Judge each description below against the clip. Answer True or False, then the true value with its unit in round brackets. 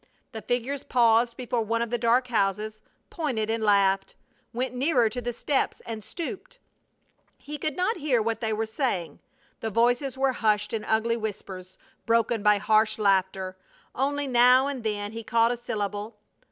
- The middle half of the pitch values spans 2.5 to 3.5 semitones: True (2.9 semitones)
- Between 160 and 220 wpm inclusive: True (165 wpm)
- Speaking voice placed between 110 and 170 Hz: False (230 Hz)